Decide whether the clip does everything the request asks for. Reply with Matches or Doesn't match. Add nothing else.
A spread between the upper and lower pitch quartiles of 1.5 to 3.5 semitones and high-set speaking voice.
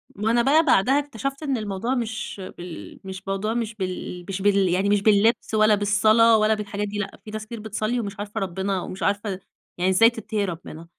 Matches